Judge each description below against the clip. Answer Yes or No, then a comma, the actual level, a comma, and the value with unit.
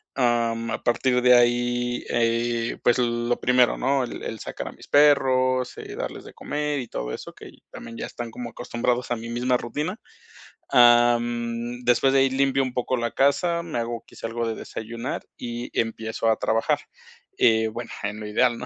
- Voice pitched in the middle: No, low, 120 Hz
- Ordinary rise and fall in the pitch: No, narrow, 1.6 semitones